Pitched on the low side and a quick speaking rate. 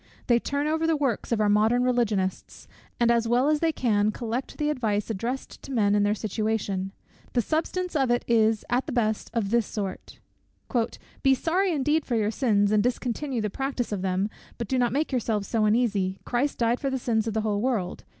No: high, 235 Hz; fast, 210 wpm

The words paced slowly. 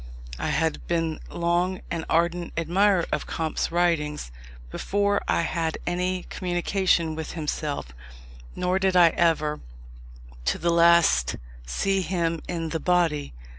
Yes: slow, 130 wpm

